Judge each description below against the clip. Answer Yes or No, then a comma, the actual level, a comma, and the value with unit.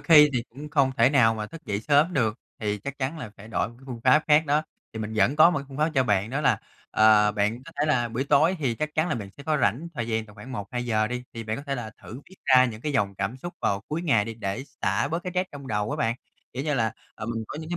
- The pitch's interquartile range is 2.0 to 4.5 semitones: No, average, 5.2 semitones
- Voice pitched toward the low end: Yes, low, 125 Hz